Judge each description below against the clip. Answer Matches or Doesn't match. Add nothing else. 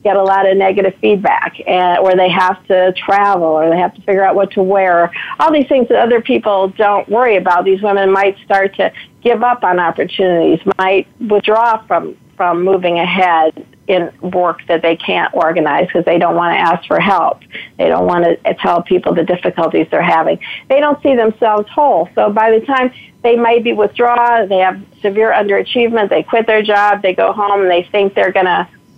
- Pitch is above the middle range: Matches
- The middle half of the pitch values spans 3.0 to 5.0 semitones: Matches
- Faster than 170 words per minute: Matches